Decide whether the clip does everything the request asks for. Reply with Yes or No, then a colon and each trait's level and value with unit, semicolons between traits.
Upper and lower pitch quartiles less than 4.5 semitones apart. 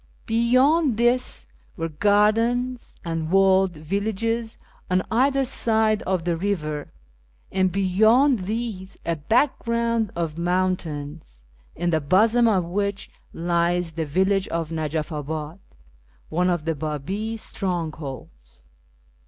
No: average, 5.3 semitones